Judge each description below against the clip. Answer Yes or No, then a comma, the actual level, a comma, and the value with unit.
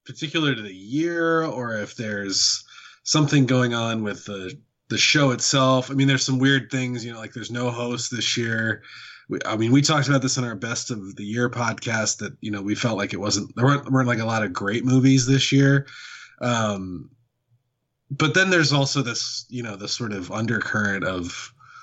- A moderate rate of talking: No, fast, 210 wpm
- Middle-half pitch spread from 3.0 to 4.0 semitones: Yes, average, 3.7 semitones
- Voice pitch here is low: Yes, low, 120 Hz